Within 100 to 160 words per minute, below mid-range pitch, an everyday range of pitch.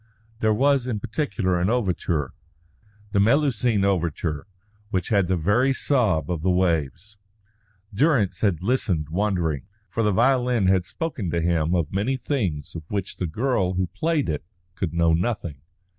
No: average, 155 wpm; very low, 95 Hz; wide, 6.0 semitones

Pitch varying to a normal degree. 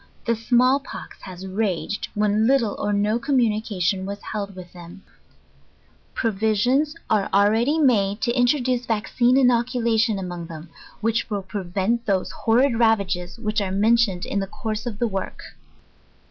Yes: average, 3.4 semitones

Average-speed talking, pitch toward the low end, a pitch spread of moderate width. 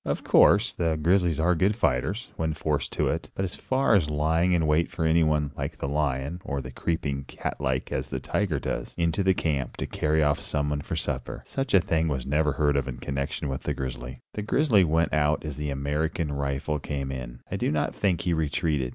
No: fast, 210 wpm; very low, 75 Hz; average, 3.2 semitones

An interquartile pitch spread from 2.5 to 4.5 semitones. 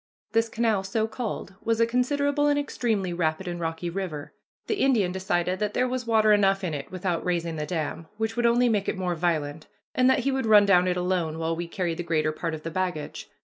No: average, 5.1 semitones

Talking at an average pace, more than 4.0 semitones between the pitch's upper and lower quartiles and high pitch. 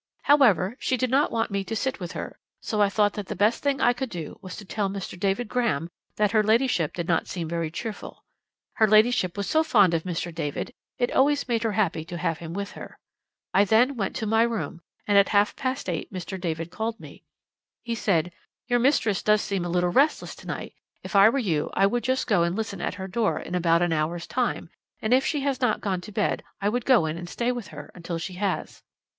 No: fast, 235 wpm; average, 5.1 semitones; high, 205 Hz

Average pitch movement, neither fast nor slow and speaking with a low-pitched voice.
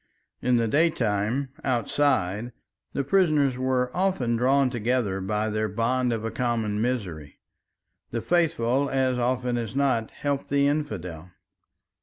No: average, 3.9 semitones; slow, 130 wpm; low, 125 Hz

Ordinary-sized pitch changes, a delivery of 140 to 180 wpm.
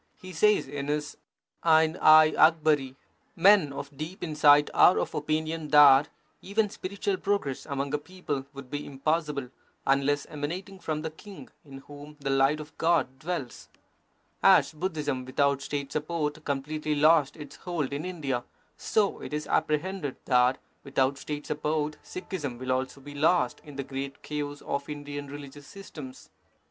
No: narrow, 2.3 semitones; average, 155 wpm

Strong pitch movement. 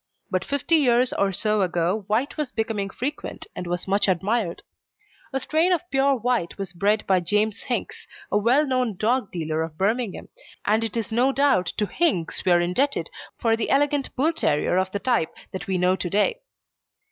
Yes: wide, 5.7 semitones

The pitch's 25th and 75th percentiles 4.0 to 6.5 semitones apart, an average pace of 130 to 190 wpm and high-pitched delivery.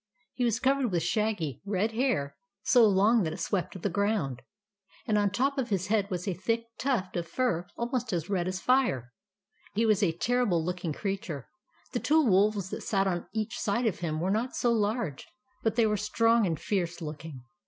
No: average, 4.7 semitones; fast, 205 wpm; high, 200 Hz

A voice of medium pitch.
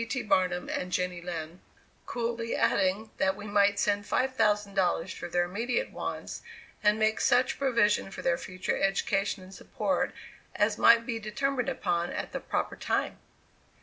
No: high, 205 Hz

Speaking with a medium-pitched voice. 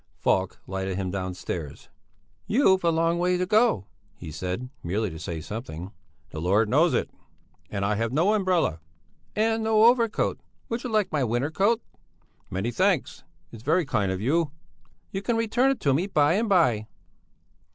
Yes: medium, 150 Hz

